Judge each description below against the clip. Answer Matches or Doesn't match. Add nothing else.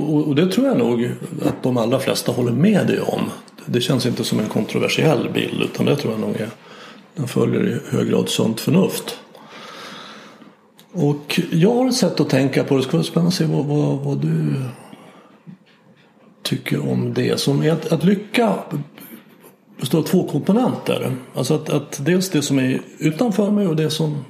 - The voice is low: Doesn't match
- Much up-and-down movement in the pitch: Matches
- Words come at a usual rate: Matches